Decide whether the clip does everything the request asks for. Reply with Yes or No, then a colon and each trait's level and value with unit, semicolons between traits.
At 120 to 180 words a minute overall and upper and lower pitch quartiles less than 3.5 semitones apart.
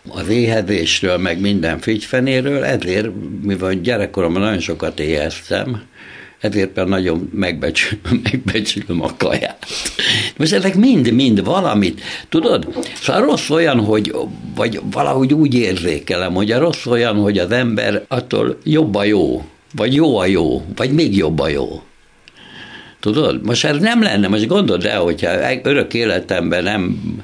No: average, 140 wpm; average, 4.3 semitones